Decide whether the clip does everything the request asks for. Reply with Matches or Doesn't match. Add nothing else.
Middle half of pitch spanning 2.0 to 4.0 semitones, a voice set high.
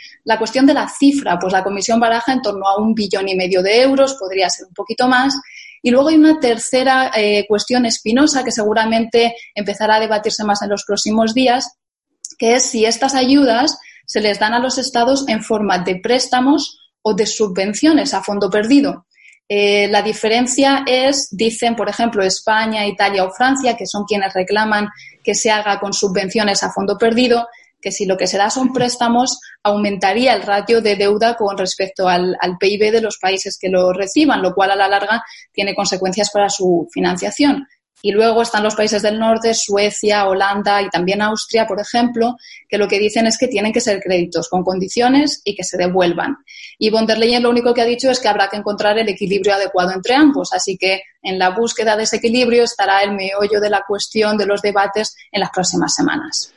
Matches